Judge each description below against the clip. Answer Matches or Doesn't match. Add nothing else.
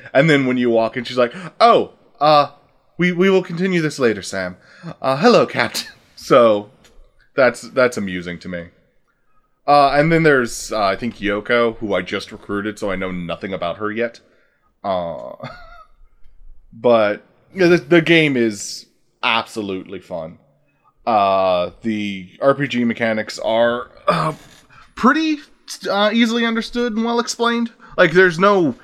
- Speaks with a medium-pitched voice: Doesn't match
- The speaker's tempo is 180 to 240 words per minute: Doesn't match